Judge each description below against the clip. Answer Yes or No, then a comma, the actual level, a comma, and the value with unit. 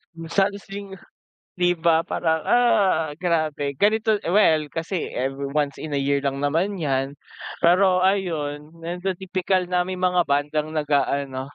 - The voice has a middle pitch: Yes, medium, 165 Hz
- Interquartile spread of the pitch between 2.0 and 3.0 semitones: No, average, 4.3 semitones